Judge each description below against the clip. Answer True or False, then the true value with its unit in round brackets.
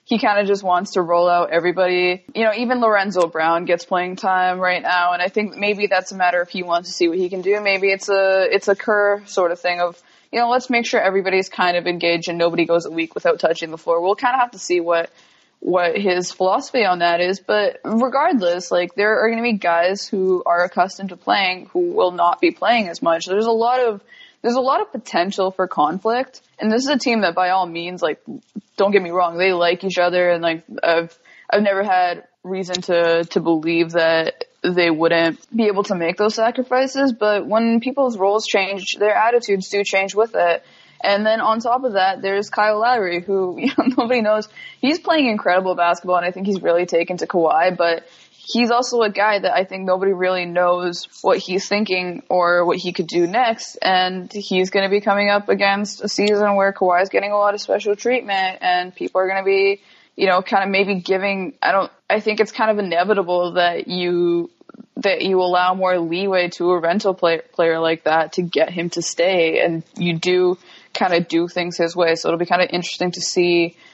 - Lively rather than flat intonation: False (3.3 semitones)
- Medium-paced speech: False (225 wpm)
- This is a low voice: False (190 Hz)